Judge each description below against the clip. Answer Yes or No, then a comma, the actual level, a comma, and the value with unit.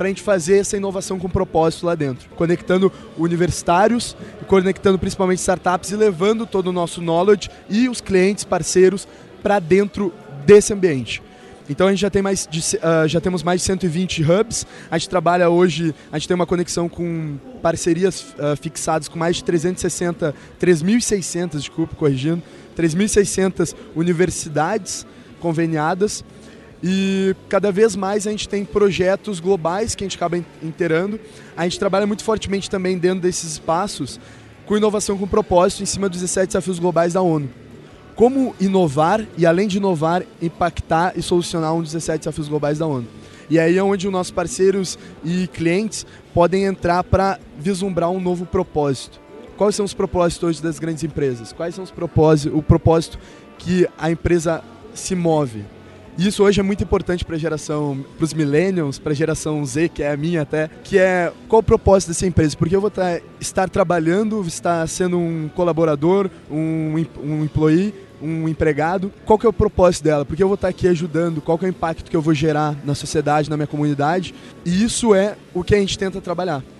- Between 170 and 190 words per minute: Yes, average, 175 wpm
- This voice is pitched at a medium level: Yes, medium, 175 Hz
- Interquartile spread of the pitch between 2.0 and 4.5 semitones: Yes, average, 3.3 semitones